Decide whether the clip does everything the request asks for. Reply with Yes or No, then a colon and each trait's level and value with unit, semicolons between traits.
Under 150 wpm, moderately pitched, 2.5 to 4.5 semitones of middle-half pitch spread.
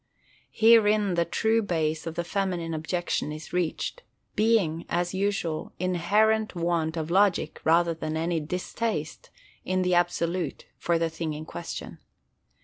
Yes: average, 140 wpm; medium, 175 Hz; average, 3.5 semitones